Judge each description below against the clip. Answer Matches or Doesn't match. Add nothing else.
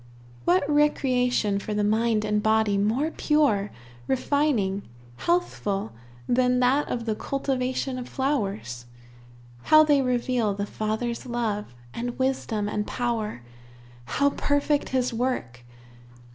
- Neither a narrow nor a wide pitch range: Matches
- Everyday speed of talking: Doesn't match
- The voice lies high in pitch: Matches